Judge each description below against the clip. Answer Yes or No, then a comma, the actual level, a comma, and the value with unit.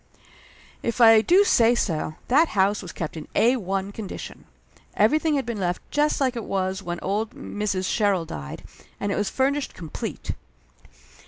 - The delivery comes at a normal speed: Yes, average, 160 wpm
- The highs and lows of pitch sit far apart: No, average, 4.6 semitones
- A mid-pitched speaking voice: No, high, 210 Hz